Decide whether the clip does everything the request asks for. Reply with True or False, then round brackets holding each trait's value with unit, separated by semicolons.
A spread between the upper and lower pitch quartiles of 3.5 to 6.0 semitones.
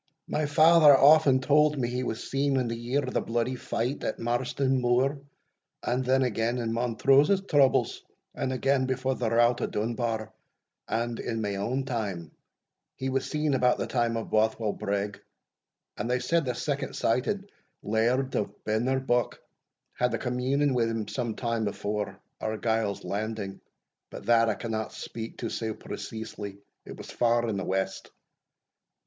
False (3.0 semitones)